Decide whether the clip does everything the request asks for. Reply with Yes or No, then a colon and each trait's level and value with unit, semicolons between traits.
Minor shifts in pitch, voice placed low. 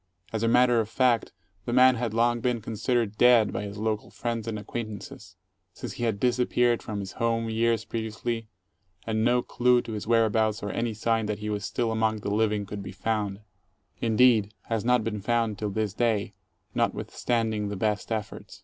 Yes: narrow, 1.9 semitones; low, 110 Hz